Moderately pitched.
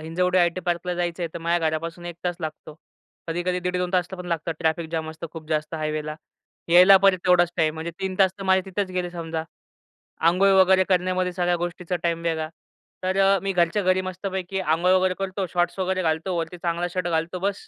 Yes: medium, 175 Hz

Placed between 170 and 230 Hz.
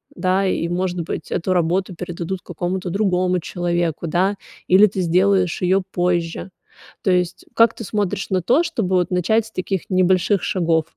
Yes: medium, 185 Hz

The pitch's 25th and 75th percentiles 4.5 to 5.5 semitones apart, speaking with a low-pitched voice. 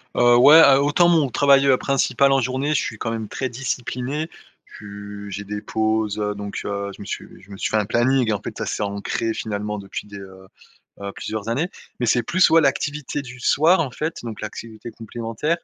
Yes: average, 4.9 semitones; low, 115 Hz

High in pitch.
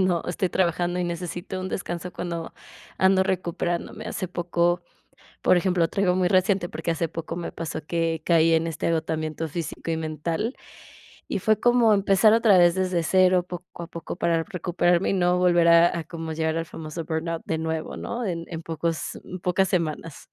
No: medium, 175 Hz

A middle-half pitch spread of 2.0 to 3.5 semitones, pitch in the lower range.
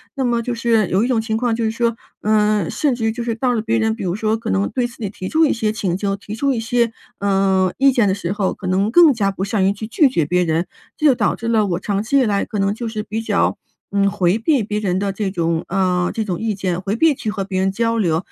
No: average, 3.2 semitones; high, 215 Hz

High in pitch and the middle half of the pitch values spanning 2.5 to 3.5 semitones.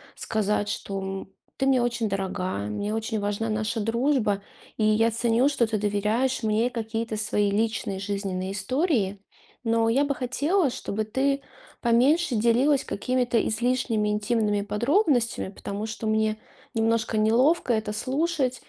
Yes: high, 225 Hz; average, 3.2 semitones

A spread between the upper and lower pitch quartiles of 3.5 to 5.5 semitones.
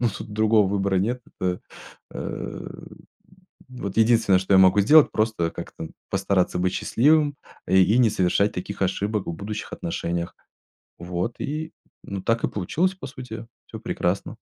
Yes: average, 4.0 semitones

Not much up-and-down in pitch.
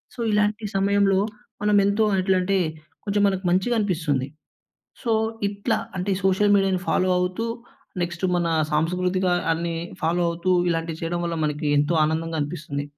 No: average, 3.2 semitones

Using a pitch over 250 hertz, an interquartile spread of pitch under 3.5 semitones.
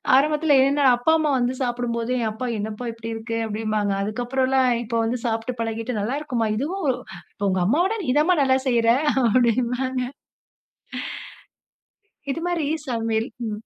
No: high, 245 Hz; average, 2.9 semitones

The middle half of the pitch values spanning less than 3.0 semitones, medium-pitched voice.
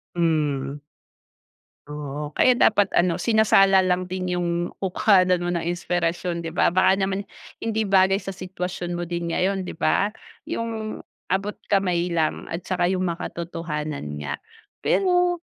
Yes: narrow, 2.4 semitones; medium, 180 Hz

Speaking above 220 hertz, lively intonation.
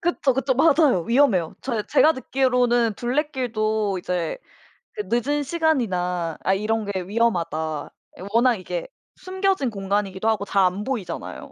Yes: high, 230 Hz; wide, 5.8 semitones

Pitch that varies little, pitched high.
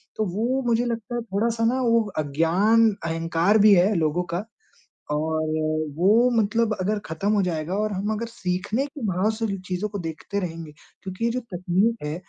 No: average, 4.7 semitones; high, 200 Hz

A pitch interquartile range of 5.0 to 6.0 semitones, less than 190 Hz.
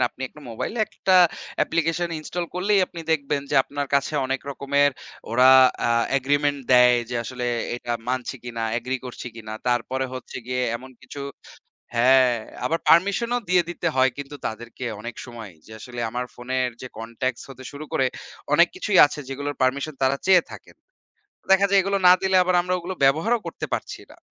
Yes: average, 5.3 semitones; low, 135 Hz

